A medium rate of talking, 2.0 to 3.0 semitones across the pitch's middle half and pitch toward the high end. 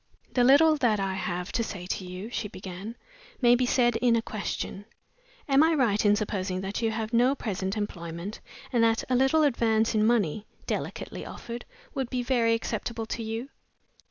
No: average, 185 wpm; average, 3.4 semitones; high, 225 Hz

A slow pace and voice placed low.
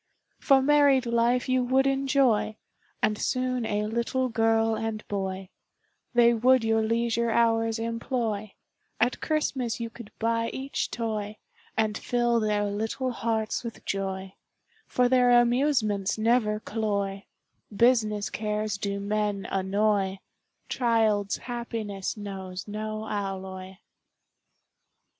No: slow, 115 wpm; high, 225 Hz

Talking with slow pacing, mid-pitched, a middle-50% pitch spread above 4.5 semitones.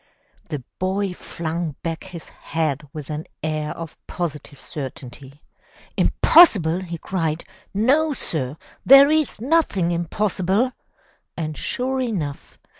Yes: slow, 115 wpm; medium, 170 Hz; wide, 5.5 semitones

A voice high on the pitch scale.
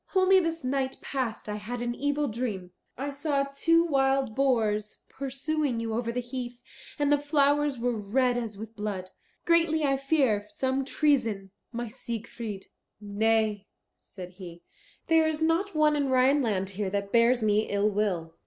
Yes: high, 245 Hz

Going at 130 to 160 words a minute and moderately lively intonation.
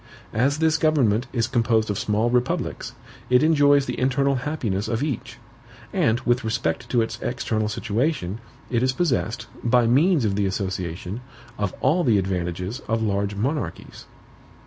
Yes: average, 150 wpm; average, 4.4 semitones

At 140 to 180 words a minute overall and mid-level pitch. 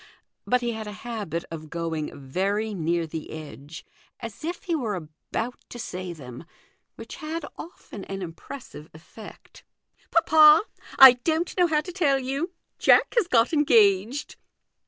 No: average, 155 wpm; high, 220 Hz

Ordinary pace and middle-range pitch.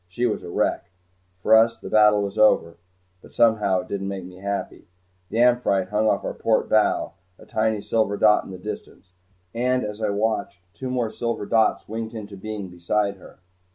No: average, 190 wpm; low, 105 Hz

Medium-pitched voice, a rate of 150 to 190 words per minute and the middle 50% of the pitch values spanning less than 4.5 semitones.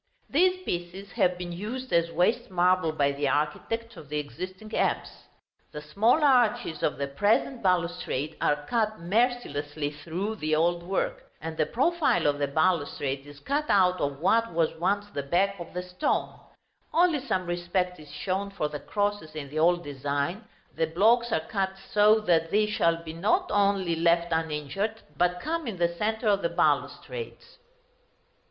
No: medium, 180 Hz; average, 170 wpm; average, 5.2 semitones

